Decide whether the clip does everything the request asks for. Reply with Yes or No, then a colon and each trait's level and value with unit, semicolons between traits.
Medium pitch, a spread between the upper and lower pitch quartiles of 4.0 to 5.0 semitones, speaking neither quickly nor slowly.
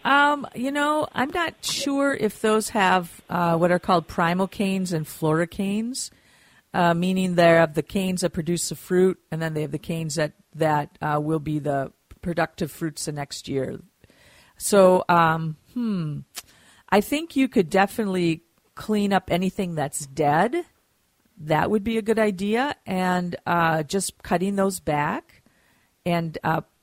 Yes: medium, 180 Hz; average, 4.4 semitones; average, 160 wpm